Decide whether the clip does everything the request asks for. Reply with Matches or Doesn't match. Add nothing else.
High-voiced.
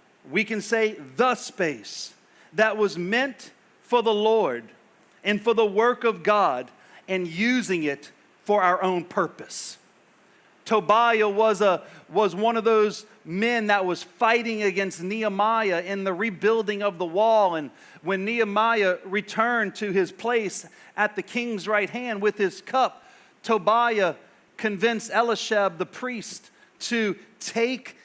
Matches